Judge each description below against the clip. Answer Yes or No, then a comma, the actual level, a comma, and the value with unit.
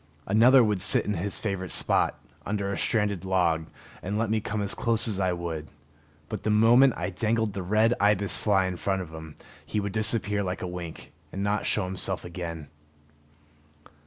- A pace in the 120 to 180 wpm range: No, average, 190 wpm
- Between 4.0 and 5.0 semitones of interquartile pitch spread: No, average, 2.9 semitones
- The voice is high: No, low, 100 Hz